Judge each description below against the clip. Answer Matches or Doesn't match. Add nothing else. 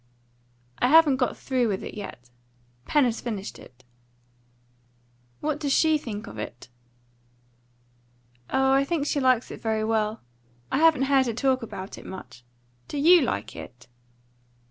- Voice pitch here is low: Doesn't match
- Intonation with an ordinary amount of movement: Matches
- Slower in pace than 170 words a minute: Matches